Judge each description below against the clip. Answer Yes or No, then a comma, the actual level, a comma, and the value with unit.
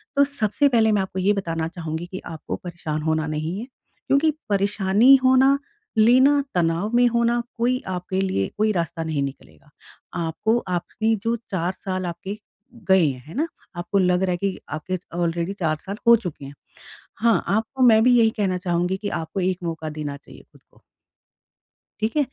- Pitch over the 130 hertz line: Yes, high, 190 Hz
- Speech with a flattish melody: No, average, 5.3 semitones